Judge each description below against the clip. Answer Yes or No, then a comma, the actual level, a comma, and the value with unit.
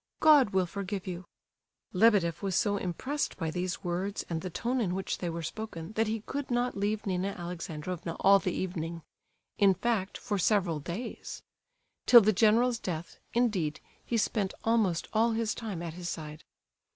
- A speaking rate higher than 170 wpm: No, average, 165 wpm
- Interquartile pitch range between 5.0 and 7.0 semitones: No, average, 4.3 semitones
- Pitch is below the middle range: No, high, 190 Hz